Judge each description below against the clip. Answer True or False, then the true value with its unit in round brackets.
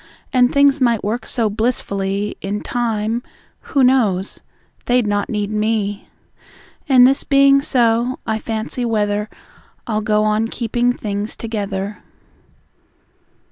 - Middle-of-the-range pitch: False (220 Hz)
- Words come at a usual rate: False (120 wpm)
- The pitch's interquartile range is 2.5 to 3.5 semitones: True (2.9 semitones)